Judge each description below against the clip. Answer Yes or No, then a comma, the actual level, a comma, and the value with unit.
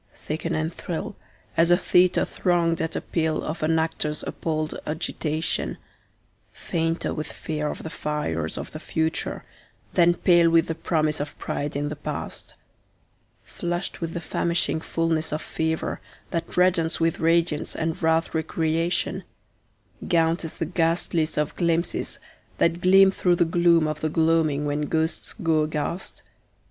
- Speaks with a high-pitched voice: No, medium, 165 Hz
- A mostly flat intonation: Yes, narrow, 1.5 semitones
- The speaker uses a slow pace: No, average, 150 wpm